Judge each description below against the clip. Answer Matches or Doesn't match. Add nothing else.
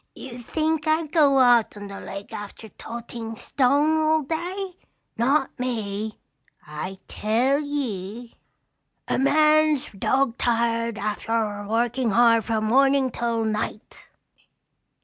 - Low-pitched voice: Doesn't match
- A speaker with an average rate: Doesn't match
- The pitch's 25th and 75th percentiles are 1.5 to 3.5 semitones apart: Doesn't match